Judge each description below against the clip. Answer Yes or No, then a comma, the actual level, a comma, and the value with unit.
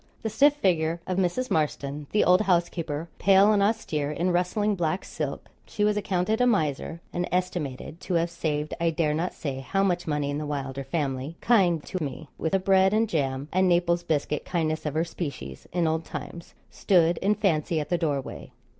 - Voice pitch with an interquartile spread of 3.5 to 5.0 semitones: Yes, average, 3.9 semitones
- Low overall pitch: No, medium, 170 Hz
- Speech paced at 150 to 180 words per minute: No, average, 195 wpm